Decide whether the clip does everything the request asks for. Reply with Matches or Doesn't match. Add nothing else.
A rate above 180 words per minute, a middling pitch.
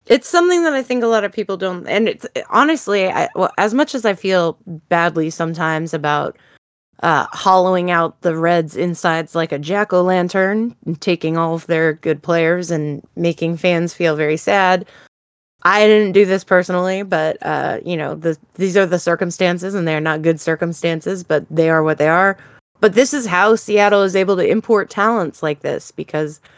Matches